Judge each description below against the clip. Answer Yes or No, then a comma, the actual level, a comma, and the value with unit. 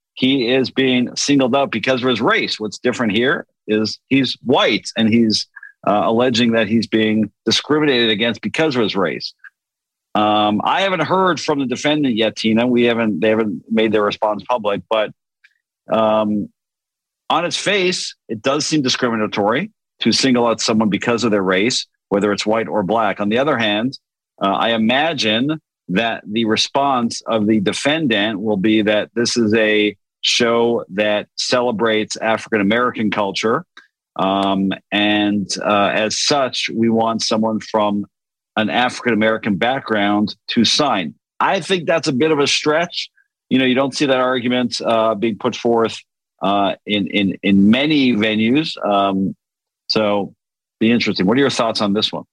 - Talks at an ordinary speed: Yes, average, 165 wpm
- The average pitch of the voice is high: No, low, 115 Hz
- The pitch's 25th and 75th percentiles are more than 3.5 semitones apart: No, average, 3.2 semitones